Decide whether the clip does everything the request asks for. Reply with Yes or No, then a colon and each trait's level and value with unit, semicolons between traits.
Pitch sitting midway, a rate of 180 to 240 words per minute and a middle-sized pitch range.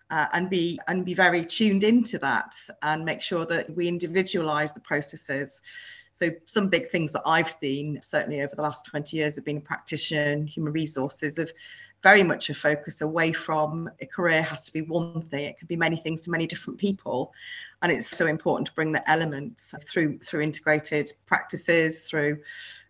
No: medium, 160 Hz; average, 190 wpm; narrow, 2.3 semitones